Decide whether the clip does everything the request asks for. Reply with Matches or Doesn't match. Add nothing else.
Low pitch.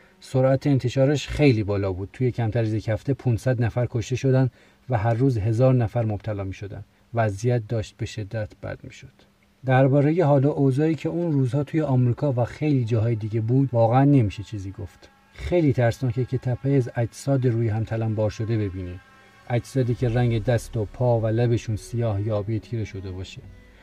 Matches